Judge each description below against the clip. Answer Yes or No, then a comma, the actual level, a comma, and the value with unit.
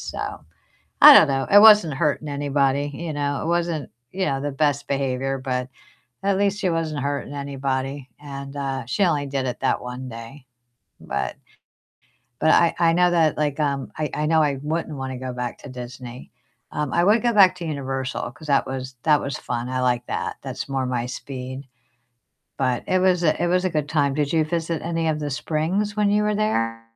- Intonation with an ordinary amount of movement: Yes, average, 3.9 semitones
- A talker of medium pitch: Yes, medium, 145 Hz